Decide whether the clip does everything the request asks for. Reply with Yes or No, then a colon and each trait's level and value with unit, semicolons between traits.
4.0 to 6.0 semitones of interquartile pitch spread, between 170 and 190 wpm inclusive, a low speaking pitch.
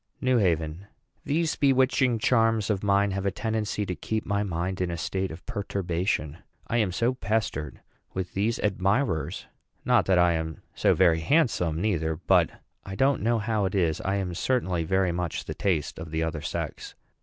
Yes: average, 4.5 semitones; average, 180 wpm; very low, 95 Hz